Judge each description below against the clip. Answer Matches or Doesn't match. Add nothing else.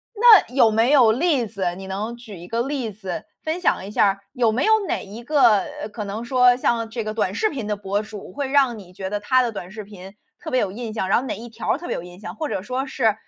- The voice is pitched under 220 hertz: Doesn't match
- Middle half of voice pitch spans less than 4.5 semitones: Matches